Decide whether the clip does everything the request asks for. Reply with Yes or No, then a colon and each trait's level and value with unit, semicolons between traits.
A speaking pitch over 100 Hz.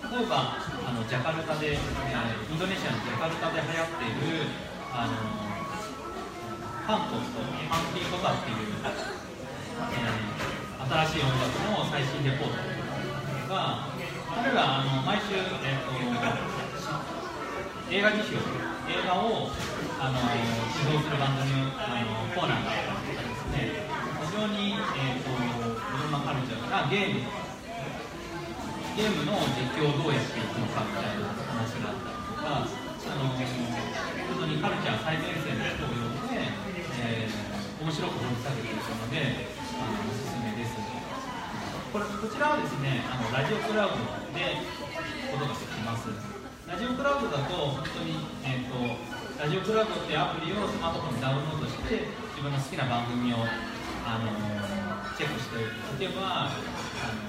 Yes: low, 135 Hz